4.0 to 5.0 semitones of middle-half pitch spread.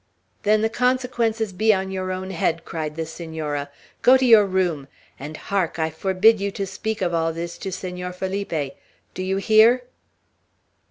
Yes: average, 4.6 semitones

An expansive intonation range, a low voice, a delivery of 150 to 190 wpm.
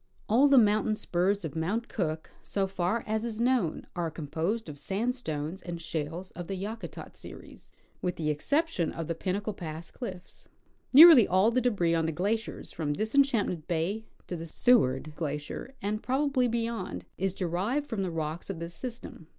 No: wide, 5.8 semitones; high, 190 Hz; average, 170 wpm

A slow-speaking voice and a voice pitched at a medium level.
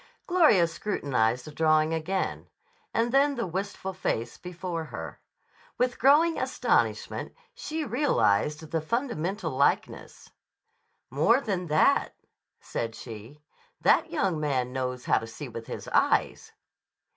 Yes: slow, 120 wpm; medium, 165 Hz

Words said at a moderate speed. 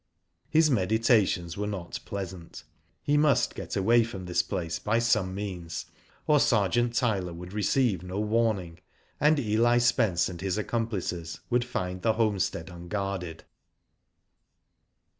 No: slow, 130 wpm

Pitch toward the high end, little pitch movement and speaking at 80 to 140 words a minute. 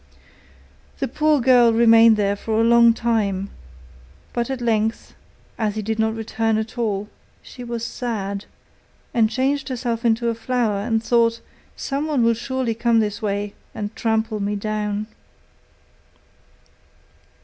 Yes: high, 225 Hz; narrow, 1.9 semitones; slow, 135 wpm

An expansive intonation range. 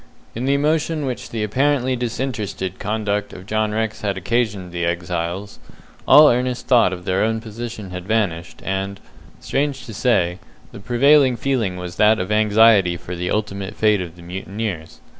No: average, 4.6 semitones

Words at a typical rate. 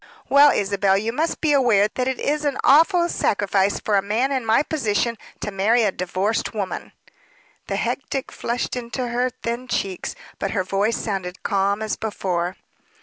Yes: average, 170 wpm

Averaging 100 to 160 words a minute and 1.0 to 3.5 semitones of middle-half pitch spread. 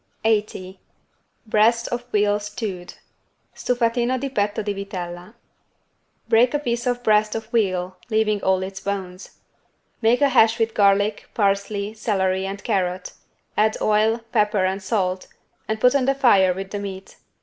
Yes: average, 150 wpm; average, 2.9 semitones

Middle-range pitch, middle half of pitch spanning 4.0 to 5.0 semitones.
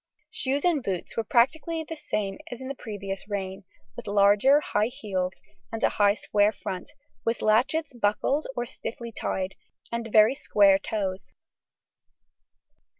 No: high, 215 Hz; average, 4.6 semitones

